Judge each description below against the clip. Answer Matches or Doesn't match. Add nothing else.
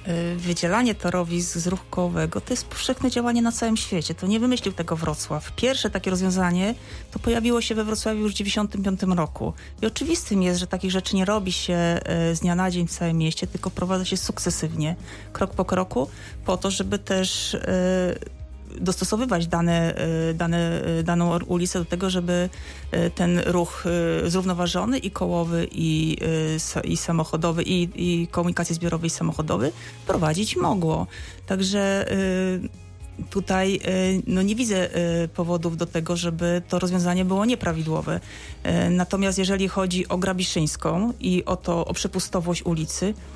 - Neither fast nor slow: Matches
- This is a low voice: Doesn't match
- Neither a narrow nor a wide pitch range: Doesn't match